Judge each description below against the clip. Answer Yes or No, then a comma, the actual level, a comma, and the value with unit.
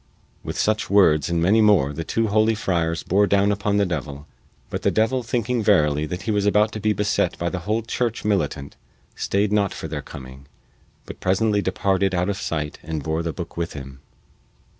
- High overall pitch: No, very low, 95 Hz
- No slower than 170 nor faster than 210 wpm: Yes, average, 200 wpm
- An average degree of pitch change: Yes, average, 4.7 semitones